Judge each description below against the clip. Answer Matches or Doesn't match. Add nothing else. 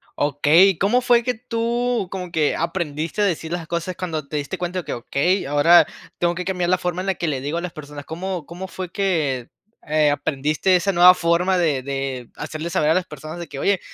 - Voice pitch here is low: Doesn't match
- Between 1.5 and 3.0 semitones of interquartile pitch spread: Doesn't match